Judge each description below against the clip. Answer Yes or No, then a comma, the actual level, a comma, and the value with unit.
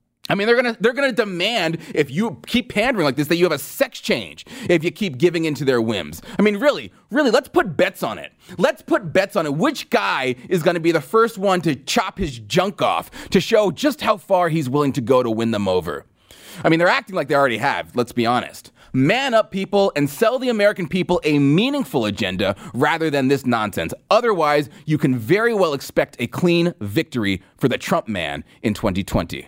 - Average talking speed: No, fast, 220 wpm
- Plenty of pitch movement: Yes, wide, 7.7 semitones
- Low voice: No, medium, 170 Hz